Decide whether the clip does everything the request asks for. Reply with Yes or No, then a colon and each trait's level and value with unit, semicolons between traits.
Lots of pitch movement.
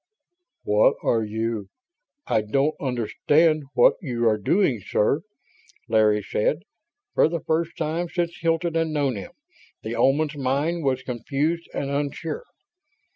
Yes: wide, 5.9 semitones